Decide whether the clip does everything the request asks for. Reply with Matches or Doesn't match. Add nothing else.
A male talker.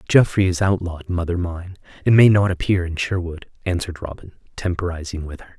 Matches